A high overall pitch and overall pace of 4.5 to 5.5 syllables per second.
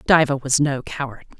No: medium, 140 Hz; 4.8 syllables/s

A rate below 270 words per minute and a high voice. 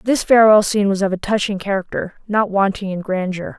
Yes: average, 200 wpm; high, 200 Hz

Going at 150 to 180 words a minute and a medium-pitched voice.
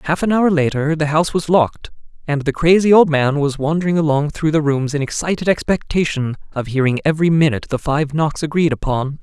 No: average, 200 wpm; medium, 155 Hz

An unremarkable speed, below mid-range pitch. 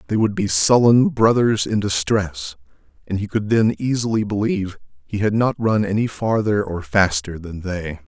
Yes: average, 170 wpm; low, 100 Hz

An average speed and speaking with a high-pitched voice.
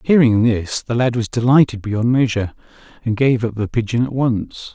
No: average, 190 wpm; low, 115 Hz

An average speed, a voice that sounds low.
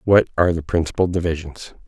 Yes: average, 160 wpm; very low, 85 Hz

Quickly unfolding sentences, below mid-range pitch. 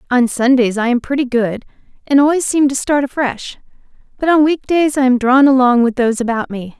No: fast, 210 wpm; very high, 260 Hz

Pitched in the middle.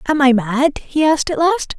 No: very high, 290 Hz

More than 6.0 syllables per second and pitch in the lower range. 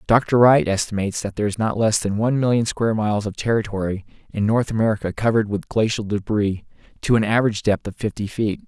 Yes: 6.4 syllables/s; low, 105 Hz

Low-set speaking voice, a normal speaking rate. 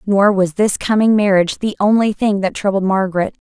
No: high, 200 Hz; average, 190 wpm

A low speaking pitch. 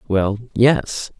Yes: low, 115 Hz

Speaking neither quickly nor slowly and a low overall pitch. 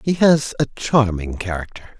Yes: average, 150 wpm; low, 115 Hz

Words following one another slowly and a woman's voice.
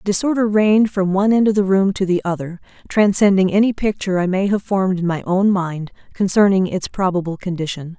No: average, 195 wpm; female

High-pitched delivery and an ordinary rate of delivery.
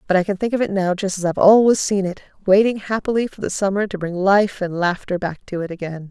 No: high, 195 Hz; fast, 265 wpm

